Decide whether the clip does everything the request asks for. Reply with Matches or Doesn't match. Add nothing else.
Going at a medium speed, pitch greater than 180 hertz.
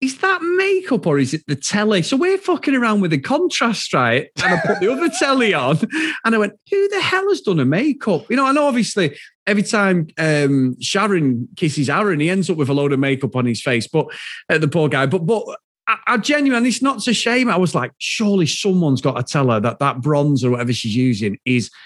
Doesn't match